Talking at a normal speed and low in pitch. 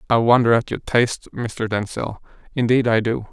Yes: average, 180 wpm; low, 115 Hz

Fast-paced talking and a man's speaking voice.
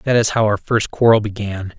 Yes: fast, 235 wpm; male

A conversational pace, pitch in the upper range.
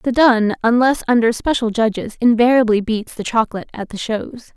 Yes: average, 170 wpm; high, 230 Hz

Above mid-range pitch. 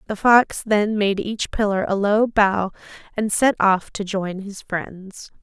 Yes: high, 205 Hz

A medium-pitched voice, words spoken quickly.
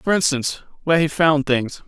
No: medium, 150 Hz; average, 190 wpm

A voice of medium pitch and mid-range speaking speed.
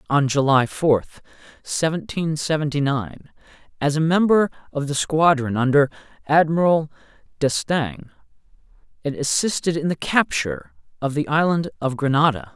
No: medium, 145 Hz; slow, 120 wpm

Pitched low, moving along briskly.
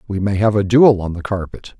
Yes: low, 100 Hz; fast, 265 wpm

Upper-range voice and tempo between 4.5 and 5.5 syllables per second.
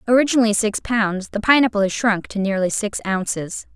Yes: high, 215 Hz; 5.4 syllables/s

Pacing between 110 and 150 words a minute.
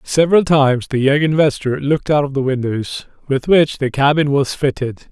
No: average, 190 wpm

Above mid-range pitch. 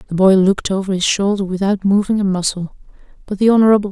Yes: high, 195 Hz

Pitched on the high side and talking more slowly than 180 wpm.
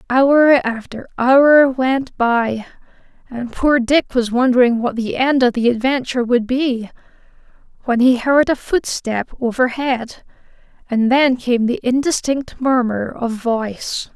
Yes: very high, 250 Hz; slow, 135 wpm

